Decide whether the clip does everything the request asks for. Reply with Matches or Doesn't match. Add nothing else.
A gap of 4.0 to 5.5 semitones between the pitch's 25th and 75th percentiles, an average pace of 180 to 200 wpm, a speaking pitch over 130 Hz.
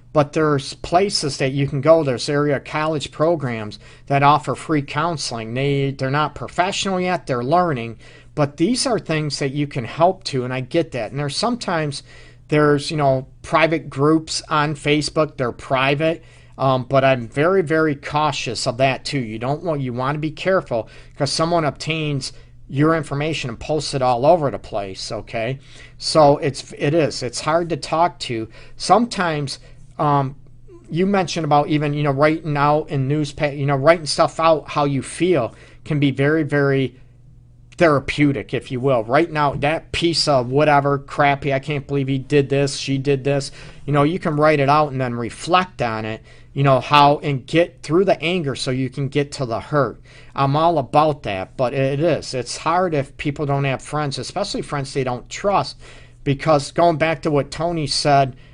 Doesn't match